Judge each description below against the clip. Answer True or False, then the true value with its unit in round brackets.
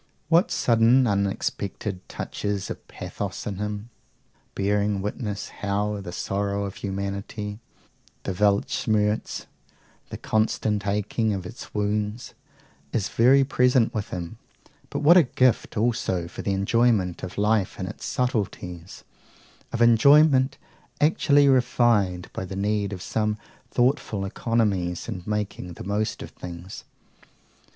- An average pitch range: True (3.0 semitones)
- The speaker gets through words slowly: True (125 wpm)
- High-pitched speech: False (105 Hz)